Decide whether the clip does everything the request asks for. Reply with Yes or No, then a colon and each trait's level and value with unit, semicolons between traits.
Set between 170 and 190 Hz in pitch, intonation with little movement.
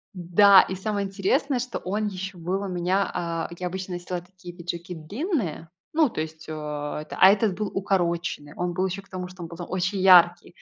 Yes: medium, 185 Hz; narrow, 2.3 semitones